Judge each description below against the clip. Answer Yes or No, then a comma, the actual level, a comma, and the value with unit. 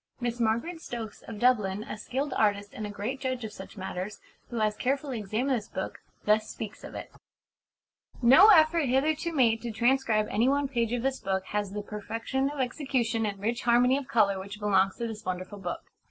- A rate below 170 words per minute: No, average, 200 wpm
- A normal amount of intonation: Yes, average, 4.0 semitones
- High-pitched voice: Yes, high, 230 Hz